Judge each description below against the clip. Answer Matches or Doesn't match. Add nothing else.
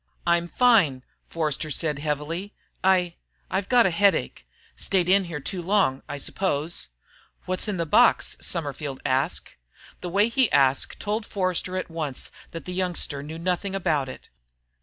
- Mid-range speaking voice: Matches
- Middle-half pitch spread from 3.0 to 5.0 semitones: Matches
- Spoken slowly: Doesn't match